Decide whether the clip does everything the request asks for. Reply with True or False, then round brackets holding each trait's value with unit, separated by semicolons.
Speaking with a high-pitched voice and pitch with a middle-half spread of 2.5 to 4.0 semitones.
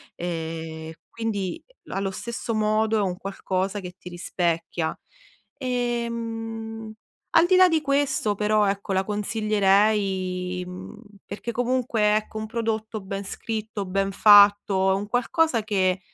True (210 Hz; 2.9 semitones)